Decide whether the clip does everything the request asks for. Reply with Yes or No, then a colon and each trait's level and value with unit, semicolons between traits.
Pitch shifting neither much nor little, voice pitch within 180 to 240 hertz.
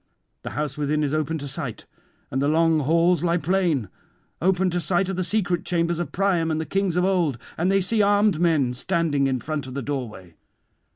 No: average, 3.9 semitones; medium, 165 Hz